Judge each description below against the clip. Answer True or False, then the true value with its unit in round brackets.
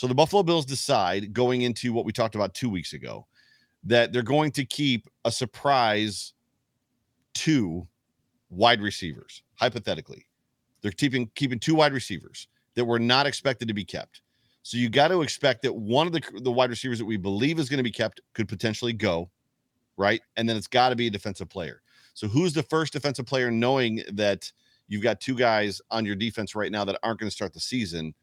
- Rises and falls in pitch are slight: False (3.4 semitones)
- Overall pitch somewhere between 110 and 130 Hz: True (120 Hz)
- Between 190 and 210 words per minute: True (200 wpm)